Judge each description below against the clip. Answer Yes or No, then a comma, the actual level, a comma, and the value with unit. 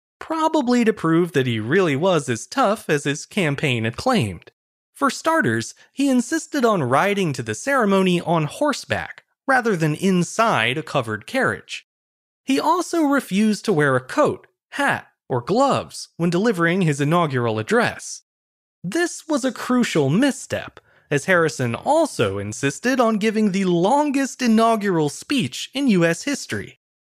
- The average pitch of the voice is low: No, high, 195 Hz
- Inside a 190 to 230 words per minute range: No, average, 140 wpm